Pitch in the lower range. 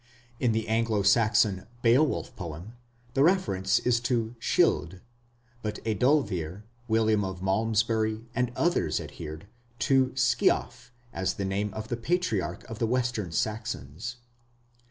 Yes: low, 110 Hz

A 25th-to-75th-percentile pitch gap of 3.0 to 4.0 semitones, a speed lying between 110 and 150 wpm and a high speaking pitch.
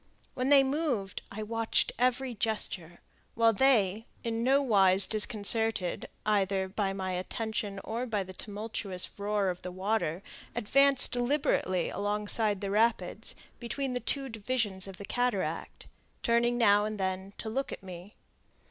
Yes: average, 3.6 semitones; average, 145 wpm; high, 215 Hz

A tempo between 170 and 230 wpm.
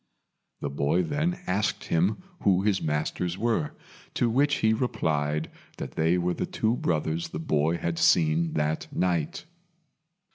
No: average, 145 wpm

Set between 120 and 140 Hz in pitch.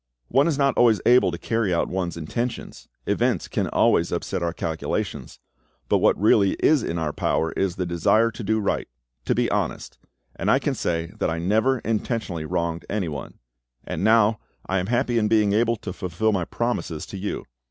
No: low, 100 Hz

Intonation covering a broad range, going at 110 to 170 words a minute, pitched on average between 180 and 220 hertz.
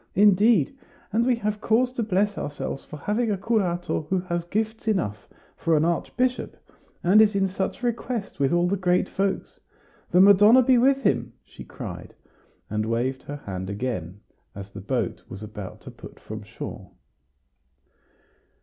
Yes: wide, 7.7 semitones; average, 160 wpm; high, 190 Hz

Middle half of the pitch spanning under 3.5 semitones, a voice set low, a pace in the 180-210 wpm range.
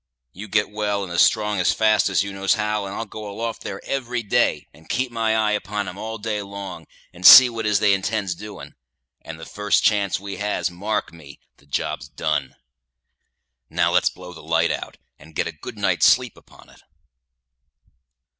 Yes: average, 2.8 semitones; low, 105 Hz; average, 190 wpm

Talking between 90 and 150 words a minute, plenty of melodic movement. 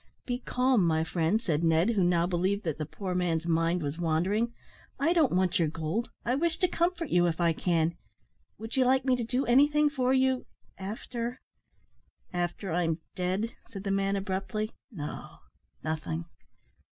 No: average, 175 wpm; wide, 6.6 semitones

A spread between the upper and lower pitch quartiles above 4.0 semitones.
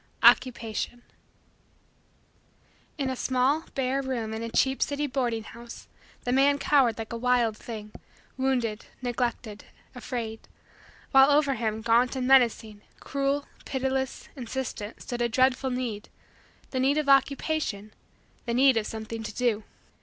No: average, 2.9 semitones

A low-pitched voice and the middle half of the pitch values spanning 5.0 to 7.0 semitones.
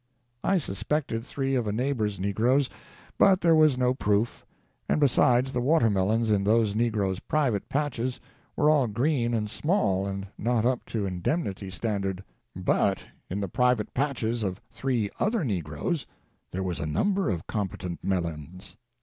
Yes: low, 115 Hz; wide, 5.5 semitones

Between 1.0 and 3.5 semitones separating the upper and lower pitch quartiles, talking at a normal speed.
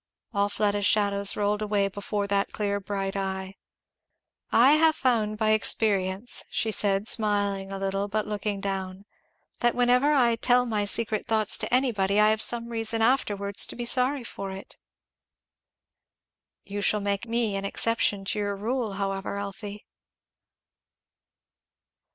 Yes: narrow, 2.4 semitones; average, 145 wpm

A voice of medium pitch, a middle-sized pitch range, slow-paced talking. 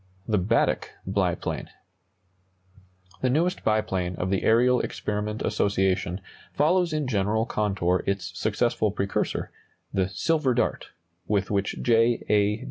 No: low, 105 Hz; average, 3.8 semitones; slow, 120 wpm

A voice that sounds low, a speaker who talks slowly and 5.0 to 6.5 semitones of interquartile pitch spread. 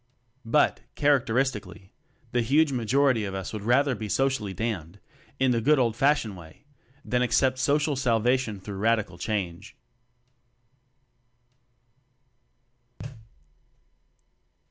No: low, 120 Hz; slow, 100 wpm; average, 4.5 semitones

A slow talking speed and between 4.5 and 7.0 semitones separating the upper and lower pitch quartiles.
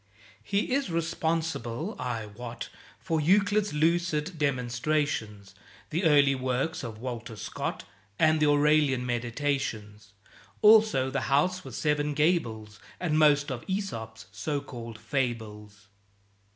Yes: slow, 115 wpm; wide, 5.6 semitones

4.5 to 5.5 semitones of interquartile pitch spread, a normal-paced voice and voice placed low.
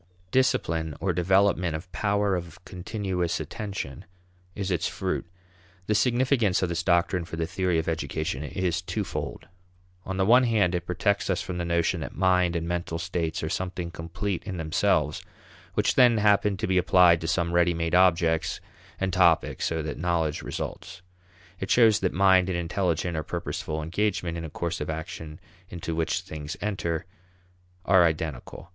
No: narrow, 2.5 semitones; average, 165 wpm; very low, 90 Hz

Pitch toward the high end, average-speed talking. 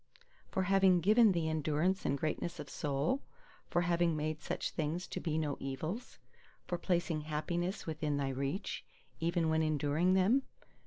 No: medium, 160 Hz; average, 155 wpm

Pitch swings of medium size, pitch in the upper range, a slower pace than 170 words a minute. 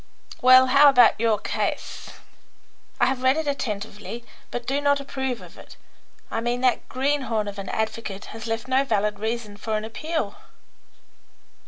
Yes: average, 3.5 semitones; high, 240 Hz; average, 160 wpm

